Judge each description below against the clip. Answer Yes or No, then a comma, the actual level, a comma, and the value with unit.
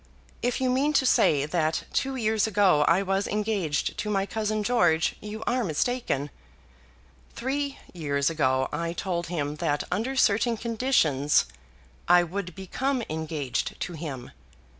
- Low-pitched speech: No, high, 195 Hz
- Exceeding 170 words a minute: No, average, 140 wpm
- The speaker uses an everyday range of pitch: No, wide, 6.7 semitones